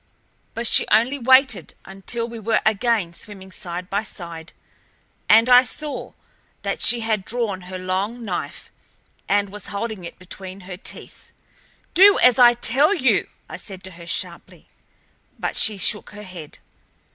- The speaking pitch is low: No, high, 210 Hz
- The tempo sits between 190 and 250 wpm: No, average, 155 wpm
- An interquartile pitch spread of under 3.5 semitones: No, average, 4.1 semitones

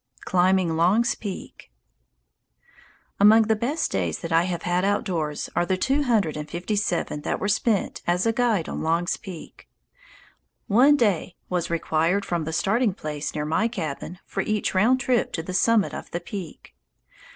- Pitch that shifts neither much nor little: Yes, average, 4.6 semitones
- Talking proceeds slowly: No, average, 170 wpm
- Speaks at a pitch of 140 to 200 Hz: Yes, medium, 185 Hz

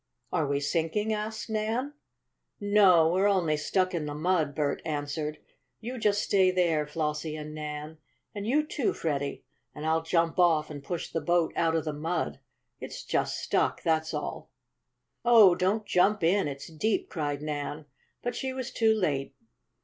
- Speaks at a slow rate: No, average, 165 wpm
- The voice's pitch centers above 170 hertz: No, medium, 165 Hz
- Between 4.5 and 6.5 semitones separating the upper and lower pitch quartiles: Yes, average, 5.1 semitones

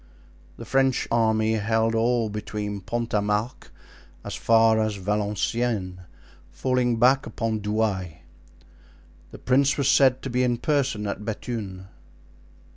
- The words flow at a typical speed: No, slow, 125 wpm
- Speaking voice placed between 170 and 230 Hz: No, low, 110 Hz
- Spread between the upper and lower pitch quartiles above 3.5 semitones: No, average, 2.8 semitones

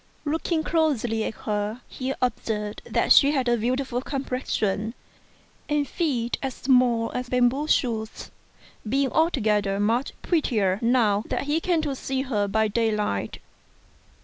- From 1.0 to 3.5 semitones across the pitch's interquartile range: No, average, 4.1 semitones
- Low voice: No, high, 245 Hz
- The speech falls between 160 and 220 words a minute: No, average, 140 wpm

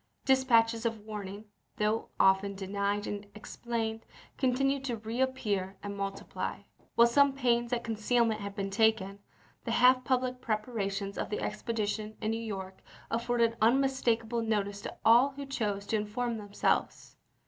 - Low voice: No, high, 225 Hz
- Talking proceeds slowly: No, average, 145 wpm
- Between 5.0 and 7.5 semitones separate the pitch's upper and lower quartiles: No, average, 2.9 semitones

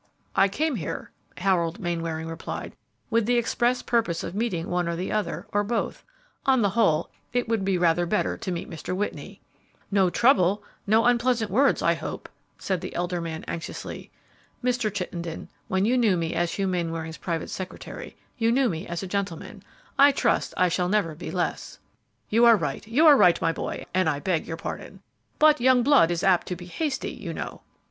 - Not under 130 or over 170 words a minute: No, average, 190 wpm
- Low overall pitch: No, high, 190 Hz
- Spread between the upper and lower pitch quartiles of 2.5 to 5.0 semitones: No, wide, 5.4 semitones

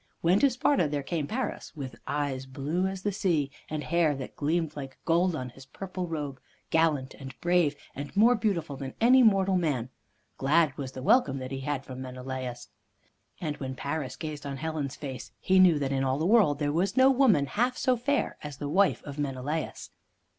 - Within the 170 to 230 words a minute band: Yes, average, 195 wpm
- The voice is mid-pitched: Yes, medium, 150 Hz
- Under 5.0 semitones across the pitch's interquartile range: No, wide, 5.4 semitones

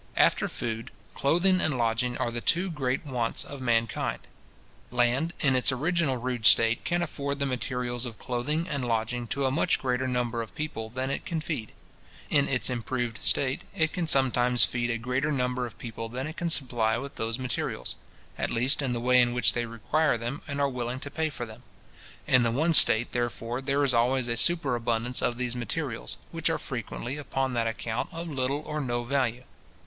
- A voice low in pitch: Yes, low, 125 Hz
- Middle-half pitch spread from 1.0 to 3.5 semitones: Yes, average, 2.9 semitones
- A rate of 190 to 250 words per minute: Yes, average, 195 wpm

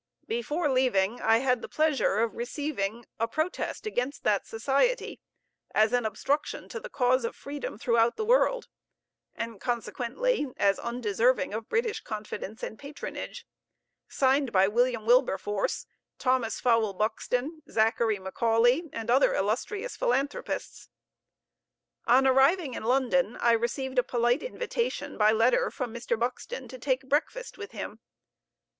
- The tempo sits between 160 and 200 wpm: No, slow, 135 wpm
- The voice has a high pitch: Yes, high, 245 Hz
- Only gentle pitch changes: No, average, 4.2 semitones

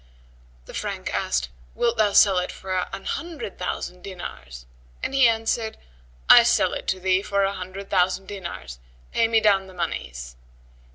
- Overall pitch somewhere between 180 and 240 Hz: Yes, high, 190 Hz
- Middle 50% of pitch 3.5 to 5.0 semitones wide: No, average, 2.9 semitones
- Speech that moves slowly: No, average, 165 wpm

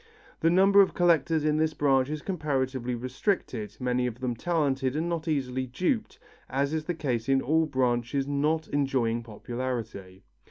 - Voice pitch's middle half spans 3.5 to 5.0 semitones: Yes, average, 4.0 semitones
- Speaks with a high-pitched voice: No, low, 135 Hz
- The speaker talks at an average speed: Yes, average, 160 wpm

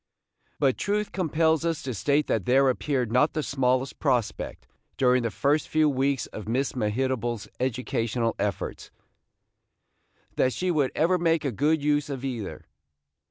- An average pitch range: Yes, average, 3.5 semitones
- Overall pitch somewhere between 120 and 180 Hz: Yes, low, 135 Hz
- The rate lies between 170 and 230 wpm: No, average, 150 wpm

